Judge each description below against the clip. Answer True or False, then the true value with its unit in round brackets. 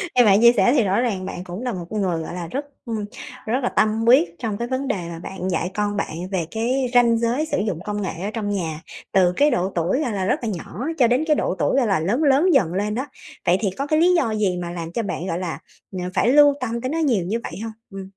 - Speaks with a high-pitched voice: True (215 Hz)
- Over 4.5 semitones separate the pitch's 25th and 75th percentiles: True (5.2 semitones)